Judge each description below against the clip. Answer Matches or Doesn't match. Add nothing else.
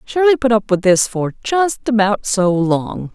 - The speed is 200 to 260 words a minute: Doesn't match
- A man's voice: Doesn't match